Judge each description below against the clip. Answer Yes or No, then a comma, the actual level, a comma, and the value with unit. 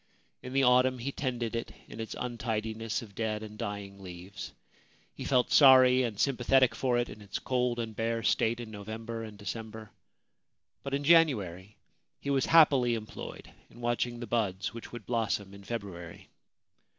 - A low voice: Yes, low, 115 Hz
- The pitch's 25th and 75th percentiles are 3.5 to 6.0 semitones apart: No, average, 2.8 semitones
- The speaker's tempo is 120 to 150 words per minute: No, average, 165 wpm